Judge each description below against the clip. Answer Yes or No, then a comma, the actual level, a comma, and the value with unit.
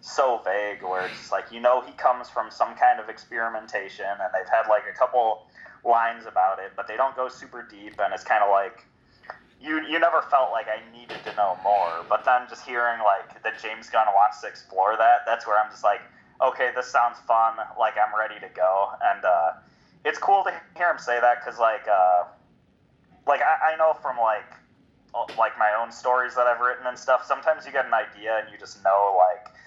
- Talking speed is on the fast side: Yes, fast, 220 wpm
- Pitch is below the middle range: Yes, low, 115 Hz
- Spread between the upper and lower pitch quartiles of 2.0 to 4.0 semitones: Yes, average, 3.0 semitones